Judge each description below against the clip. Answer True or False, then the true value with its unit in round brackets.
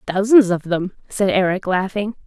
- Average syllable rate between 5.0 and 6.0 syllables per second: False (4.7 syllables/s)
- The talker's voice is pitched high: True (195 Hz)